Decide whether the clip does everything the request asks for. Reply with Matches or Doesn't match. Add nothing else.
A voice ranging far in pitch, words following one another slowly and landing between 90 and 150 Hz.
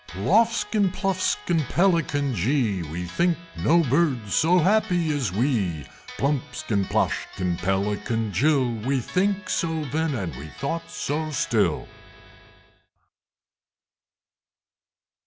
Matches